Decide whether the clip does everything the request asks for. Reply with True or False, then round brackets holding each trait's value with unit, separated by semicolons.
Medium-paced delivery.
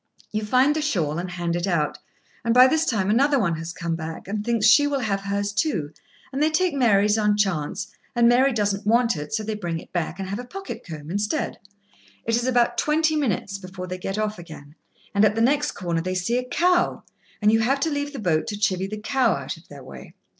False (240 wpm)